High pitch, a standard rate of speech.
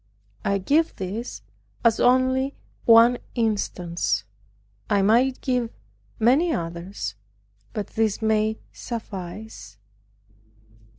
No: high, 220 Hz; slow, 85 wpm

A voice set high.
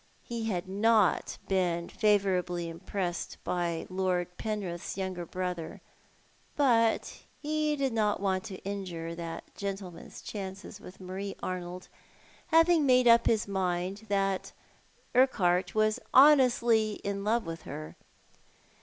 Yes: high, 195 Hz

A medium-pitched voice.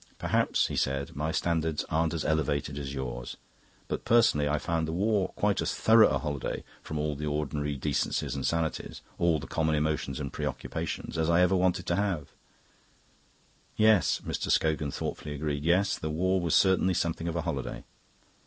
No: very low, 80 Hz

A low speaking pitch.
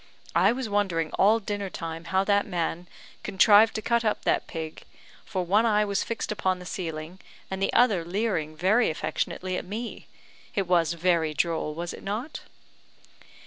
No: high, 190 Hz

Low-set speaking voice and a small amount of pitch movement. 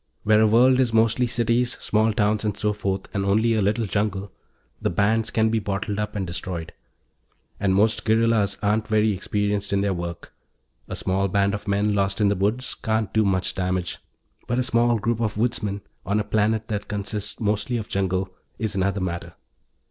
Yes: low, 105 Hz; narrow, 2.1 semitones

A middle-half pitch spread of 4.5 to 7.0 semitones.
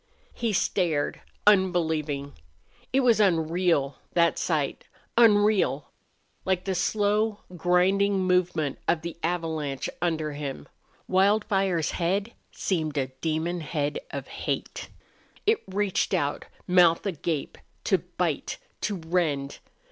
No: average, 3.9 semitones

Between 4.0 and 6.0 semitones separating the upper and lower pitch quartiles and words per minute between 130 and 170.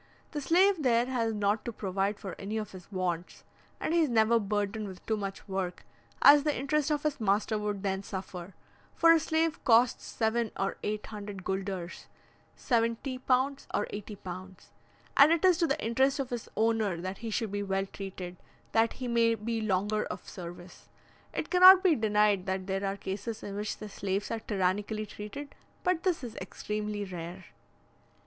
No: average, 4.4 semitones; average, 180 wpm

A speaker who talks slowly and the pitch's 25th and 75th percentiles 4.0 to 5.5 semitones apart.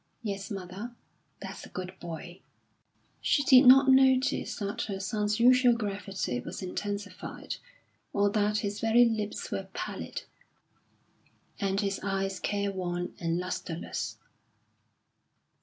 No: slow, 115 wpm; average, 3.0 semitones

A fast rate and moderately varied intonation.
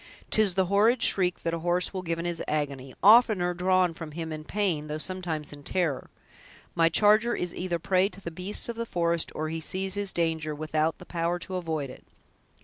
Yes: fast, 215 wpm; average, 3.0 semitones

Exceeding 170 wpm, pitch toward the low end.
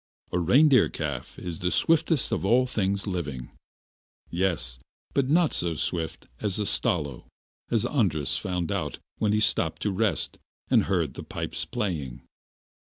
No: average, 150 wpm; very low, 90 Hz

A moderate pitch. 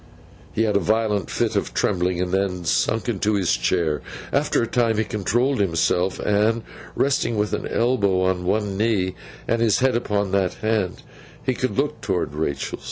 No: low, 105 Hz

